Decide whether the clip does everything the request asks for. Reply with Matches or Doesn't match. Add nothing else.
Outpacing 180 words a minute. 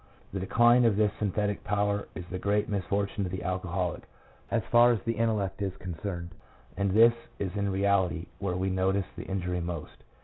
Matches